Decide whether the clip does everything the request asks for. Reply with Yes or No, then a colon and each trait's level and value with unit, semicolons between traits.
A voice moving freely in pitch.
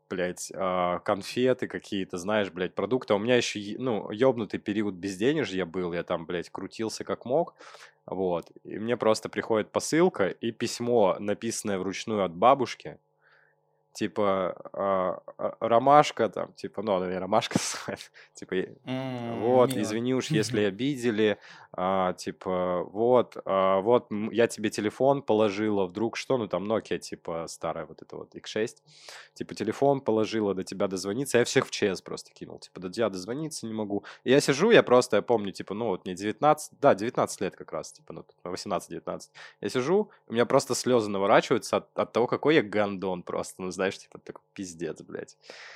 No: average, 4.1 semitones